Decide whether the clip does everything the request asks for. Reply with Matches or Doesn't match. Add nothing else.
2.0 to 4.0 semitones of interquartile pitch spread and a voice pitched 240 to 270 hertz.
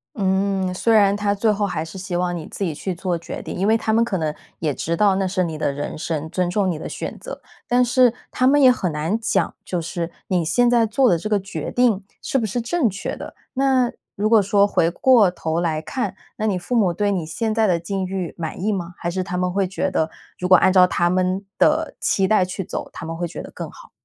Doesn't match